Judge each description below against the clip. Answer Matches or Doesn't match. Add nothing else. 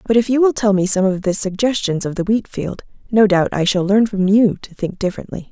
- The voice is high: Matches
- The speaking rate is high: Matches